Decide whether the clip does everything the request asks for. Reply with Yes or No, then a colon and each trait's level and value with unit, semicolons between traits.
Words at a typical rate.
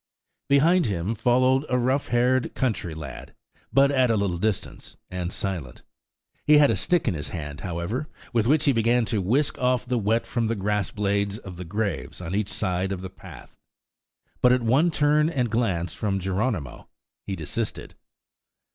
Yes: average, 175 wpm